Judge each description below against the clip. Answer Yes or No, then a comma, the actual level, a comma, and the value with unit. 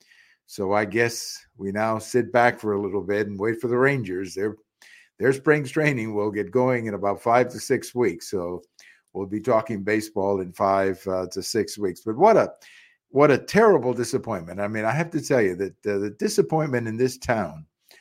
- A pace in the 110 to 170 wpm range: No, fast, 205 wpm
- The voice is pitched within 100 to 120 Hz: Yes, low, 110 Hz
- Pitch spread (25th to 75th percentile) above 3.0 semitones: Yes, average, 3.7 semitones